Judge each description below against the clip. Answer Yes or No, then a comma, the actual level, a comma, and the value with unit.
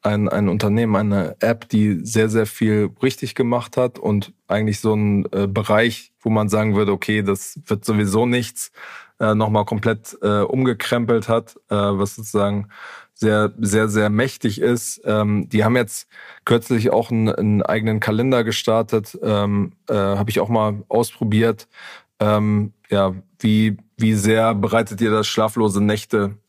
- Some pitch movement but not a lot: No, narrow, 1.6 semitones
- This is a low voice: Yes, low, 110 Hz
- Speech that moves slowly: No, average, 155 wpm